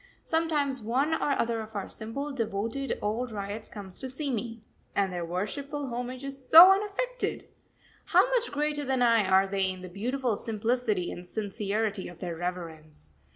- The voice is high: Yes, high, 225 Hz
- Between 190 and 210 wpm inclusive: No, average, 165 wpm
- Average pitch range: No, wide, 5.7 semitones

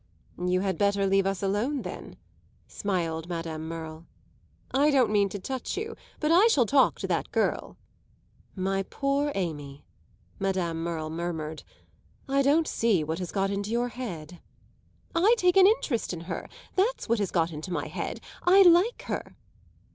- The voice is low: No, high, 195 Hz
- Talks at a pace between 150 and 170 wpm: Yes, average, 160 wpm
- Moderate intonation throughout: No, wide, 8.5 semitones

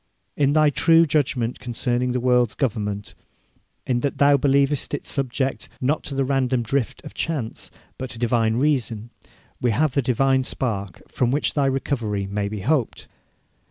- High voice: No, low, 125 Hz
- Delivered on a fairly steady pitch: No, average, 3.4 semitones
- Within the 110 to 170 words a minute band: Yes, average, 160 wpm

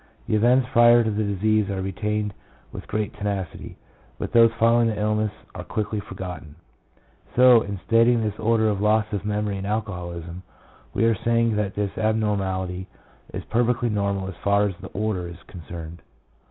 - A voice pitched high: No, low, 105 Hz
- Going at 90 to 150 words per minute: No, average, 170 wpm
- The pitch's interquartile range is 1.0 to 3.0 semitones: Yes, narrow, 2.6 semitones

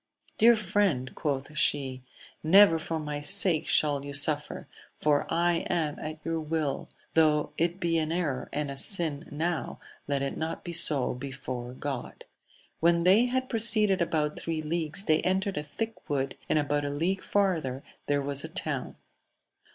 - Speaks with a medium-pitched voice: Yes, medium, 155 Hz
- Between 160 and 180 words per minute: Yes, average, 165 wpm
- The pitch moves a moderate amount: Yes, average, 3.3 semitones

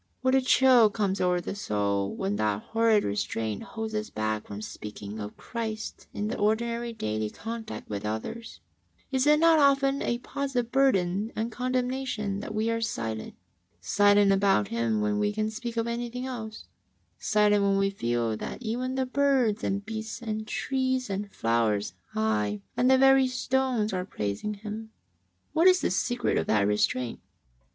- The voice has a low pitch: No, high, 215 Hz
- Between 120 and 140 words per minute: No, average, 170 wpm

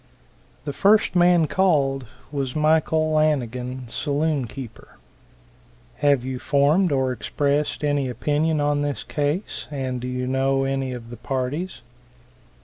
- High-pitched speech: No, medium, 140 Hz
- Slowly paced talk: Yes, slow, 130 wpm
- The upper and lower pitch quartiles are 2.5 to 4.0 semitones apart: Yes, average, 2.9 semitones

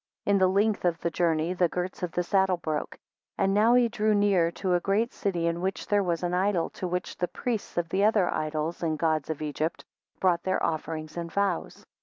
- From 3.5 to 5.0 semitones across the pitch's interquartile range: No, average, 3.0 semitones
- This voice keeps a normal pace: No, fast, 230 wpm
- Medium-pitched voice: Yes, medium, 180 Hz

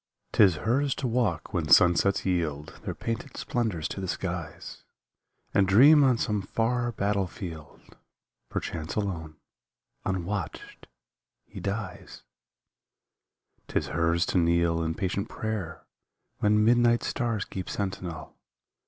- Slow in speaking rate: Yes, slow, 120 wpm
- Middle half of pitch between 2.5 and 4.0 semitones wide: No, average, 4.9 semitones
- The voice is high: No, very low, 95 Hz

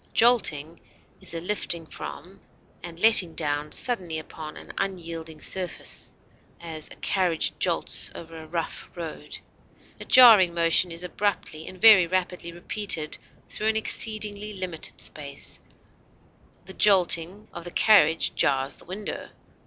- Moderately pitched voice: Yes, medium, 175 Hz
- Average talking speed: No, slow, 130 wpm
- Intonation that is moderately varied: Yes, average, 3.7 semitones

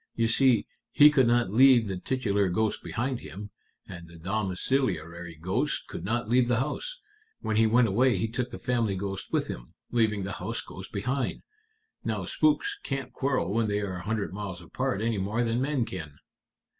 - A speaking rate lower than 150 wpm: No, average, 185 wpm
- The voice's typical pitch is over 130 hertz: No, low, 110 Hz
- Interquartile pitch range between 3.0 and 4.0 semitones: No, average, 4.6 semitones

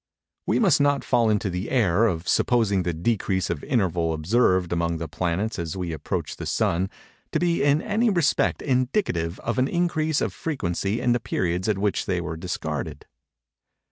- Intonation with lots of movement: Yes, wide, 7.1 semitones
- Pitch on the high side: No, low, 100 Hz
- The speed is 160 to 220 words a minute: Yes, average, 175 wpm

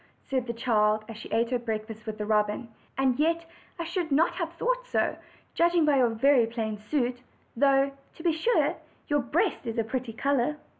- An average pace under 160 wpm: No, average, 195 wpm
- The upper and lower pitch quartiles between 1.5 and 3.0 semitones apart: No, average, 5.3 semitones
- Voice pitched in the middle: No, very high, 255 Hz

